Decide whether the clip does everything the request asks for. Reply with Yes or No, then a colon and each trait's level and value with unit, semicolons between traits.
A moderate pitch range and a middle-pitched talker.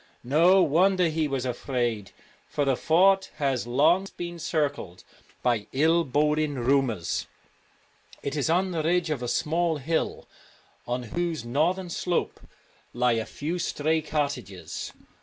Yes: average, 5.0 semitones; medium, 150 Hz